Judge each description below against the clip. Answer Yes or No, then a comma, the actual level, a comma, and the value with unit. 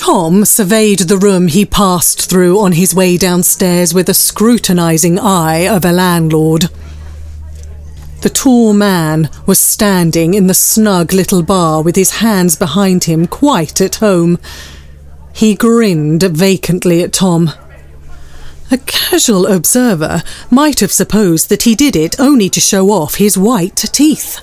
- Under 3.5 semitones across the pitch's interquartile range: No, average, 4.0 semitones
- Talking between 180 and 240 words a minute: No, average, 140 wpm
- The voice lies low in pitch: No, medium, 185 Hz